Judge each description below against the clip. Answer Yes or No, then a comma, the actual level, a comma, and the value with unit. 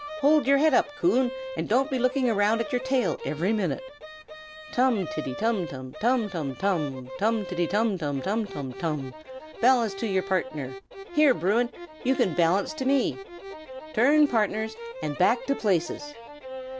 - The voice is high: Yes, high, 215 Hz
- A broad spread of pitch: Yes, wide, 6.9 semitones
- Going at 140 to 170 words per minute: Yes, average, 160 wpm